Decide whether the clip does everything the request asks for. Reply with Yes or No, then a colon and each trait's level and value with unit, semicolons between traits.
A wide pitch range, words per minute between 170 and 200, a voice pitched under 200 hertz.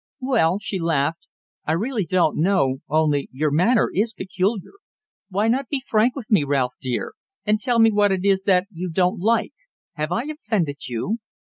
Yes: wide, 5.8 semitones; average, 180 wpm; high, 190 Hz